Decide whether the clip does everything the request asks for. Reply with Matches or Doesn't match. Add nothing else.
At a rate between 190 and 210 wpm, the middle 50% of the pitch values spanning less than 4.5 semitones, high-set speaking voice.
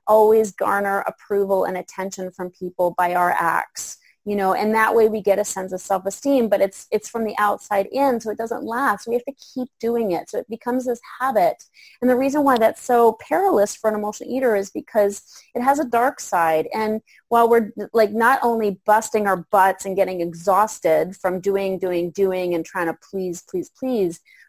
Matches